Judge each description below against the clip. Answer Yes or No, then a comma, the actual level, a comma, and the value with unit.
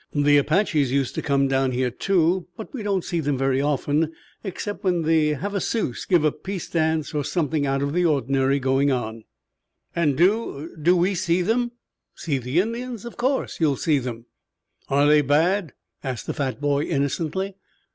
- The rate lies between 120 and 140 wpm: No, average, 180 wpm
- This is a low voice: No, medium, 150 Hz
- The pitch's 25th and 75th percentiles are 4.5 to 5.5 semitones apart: Yes, average, 4.9 semitones